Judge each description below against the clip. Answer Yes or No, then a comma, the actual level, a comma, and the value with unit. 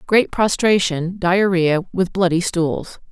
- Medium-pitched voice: Yes, medium, 180 Hz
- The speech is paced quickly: No, slow, 115 wpm